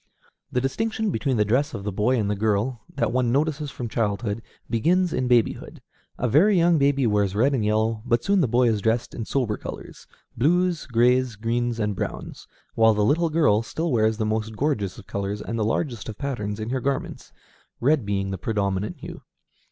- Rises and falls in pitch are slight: No, average, 4.6 semitones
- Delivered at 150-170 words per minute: No, average, 200 wpm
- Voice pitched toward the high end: No, low, 115 Hz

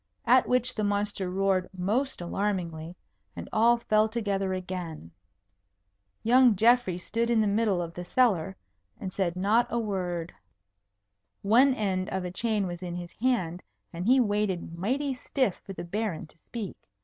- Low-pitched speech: No, high, 200 Hz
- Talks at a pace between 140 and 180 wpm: Yes, average, 160 wpm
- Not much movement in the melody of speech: No, average, 4.4 semitones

